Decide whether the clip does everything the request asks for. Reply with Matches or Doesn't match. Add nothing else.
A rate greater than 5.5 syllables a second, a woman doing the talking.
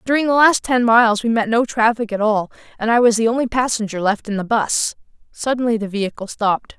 Matches